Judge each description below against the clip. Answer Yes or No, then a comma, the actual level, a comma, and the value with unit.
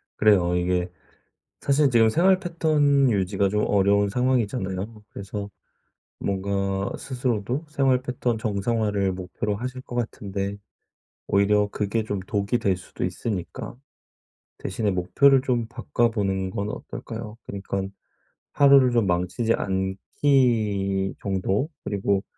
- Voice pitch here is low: Yes, low, 105 Hz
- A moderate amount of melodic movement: Yes, average, 4.1 semitones